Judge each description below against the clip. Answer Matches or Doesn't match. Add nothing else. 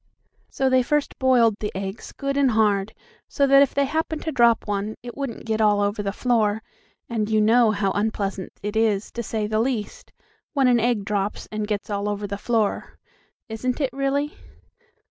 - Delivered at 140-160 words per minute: Doesn't match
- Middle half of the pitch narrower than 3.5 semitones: Doesn't match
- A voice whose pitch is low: Doesn't match